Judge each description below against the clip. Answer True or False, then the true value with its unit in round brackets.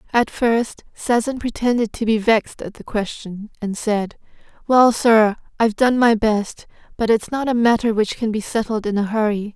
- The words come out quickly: False (190 wpm)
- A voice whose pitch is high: True (220 Hz)